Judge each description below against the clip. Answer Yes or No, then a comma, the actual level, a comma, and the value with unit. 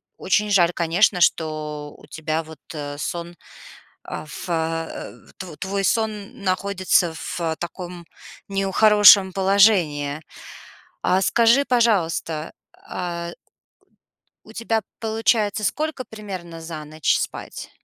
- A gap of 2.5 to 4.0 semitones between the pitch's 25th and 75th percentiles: No, average, 4.4 semitones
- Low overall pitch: No, medium, 185 Hz